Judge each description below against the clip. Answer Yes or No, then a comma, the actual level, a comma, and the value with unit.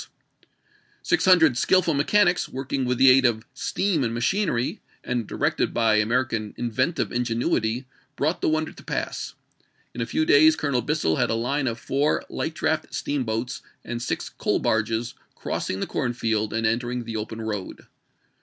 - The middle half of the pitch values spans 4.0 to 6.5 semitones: Yes, average, 4.5 semitones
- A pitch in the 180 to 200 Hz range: No, low, 125 Hz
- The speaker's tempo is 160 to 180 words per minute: Yes, average, 165 wpm